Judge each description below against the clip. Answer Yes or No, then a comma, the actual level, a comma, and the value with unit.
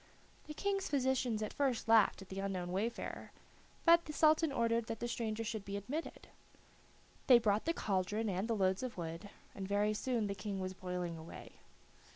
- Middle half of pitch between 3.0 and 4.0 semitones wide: No, average, 4.5 semitones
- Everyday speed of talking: Yes, average, 185 wpm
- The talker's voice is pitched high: Yes, high, 215 Hz